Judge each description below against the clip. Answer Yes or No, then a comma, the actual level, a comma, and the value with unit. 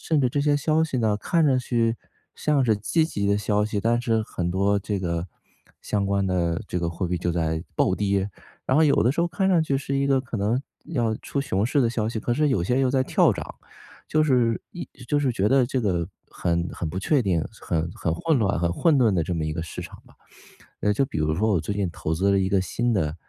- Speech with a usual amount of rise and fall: No, wide, 6.4 semitones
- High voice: No, low, 105 Hz